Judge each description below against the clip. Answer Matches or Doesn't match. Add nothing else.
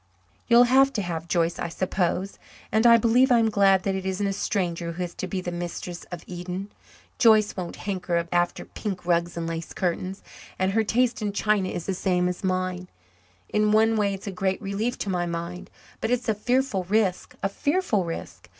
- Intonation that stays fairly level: Doesn't match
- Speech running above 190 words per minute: Matches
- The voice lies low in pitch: Doesn't match